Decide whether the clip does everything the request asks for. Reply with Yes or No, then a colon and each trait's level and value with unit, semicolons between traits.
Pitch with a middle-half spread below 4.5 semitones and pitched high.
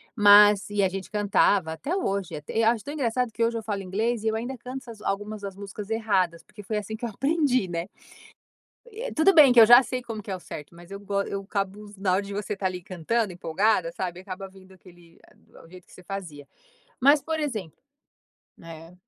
Yes: average, 3.7 semitones; high, 205 Hz